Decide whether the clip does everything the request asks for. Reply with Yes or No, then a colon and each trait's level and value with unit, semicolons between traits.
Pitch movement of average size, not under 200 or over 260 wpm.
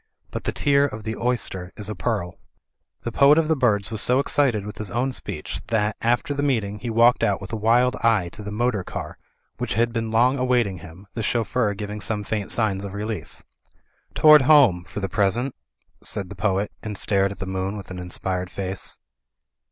Yes: average, 3.7 semitones; fast, 205 wpm